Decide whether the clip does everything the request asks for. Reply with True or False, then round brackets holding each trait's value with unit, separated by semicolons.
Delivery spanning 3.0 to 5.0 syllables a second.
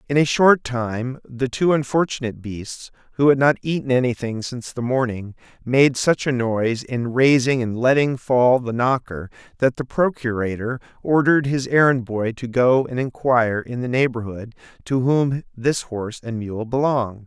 True (4.8 syllables/s)